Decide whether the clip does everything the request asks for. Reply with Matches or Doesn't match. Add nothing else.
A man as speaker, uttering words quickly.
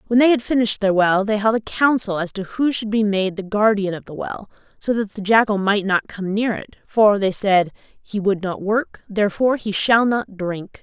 Doesn't match